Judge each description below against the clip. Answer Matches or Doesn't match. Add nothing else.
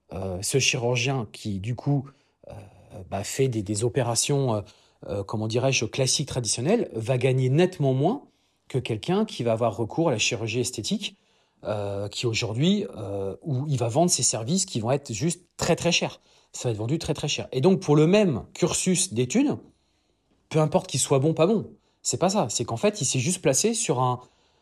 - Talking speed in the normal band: Matches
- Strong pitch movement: Matches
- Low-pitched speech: Matches